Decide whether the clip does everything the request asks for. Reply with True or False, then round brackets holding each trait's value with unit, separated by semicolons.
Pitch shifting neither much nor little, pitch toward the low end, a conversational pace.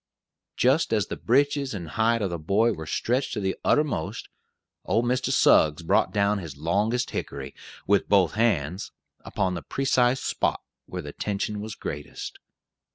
False (5.8 semitones; 105 Hz; 160 wpm)